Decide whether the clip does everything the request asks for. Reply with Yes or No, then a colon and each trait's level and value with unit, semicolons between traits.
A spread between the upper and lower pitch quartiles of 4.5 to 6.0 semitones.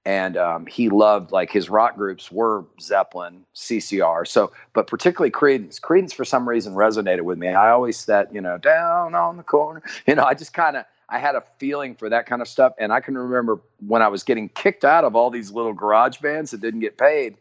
Yes: average, 4.9 semitones